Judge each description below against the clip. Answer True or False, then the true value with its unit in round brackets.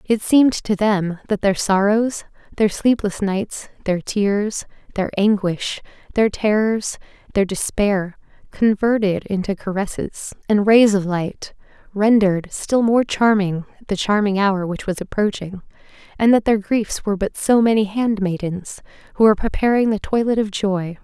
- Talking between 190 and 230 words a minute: False (145 wpm)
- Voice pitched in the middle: False (205 Hz)